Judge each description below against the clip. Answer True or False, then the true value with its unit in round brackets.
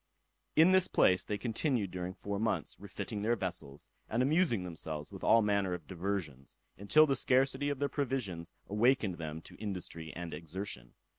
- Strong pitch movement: True (6.5 semitones)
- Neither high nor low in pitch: False (100 Hz)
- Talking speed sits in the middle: True (165 wpm)